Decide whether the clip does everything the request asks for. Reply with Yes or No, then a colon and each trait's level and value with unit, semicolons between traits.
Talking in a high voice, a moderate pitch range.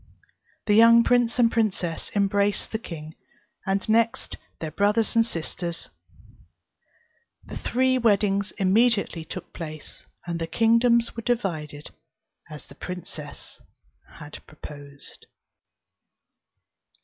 No: high, 200 Hz; wide, 5.8 semitones